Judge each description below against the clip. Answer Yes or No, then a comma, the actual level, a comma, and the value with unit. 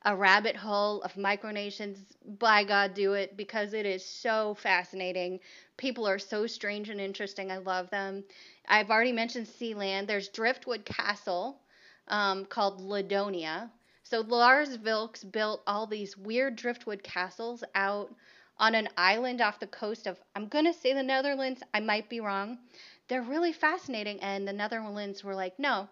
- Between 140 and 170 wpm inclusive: Yes, average, 155 wpm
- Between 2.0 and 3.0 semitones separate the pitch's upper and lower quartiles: Yes, average, 2.7 semitones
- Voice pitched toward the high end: Yes, high, 210 Hz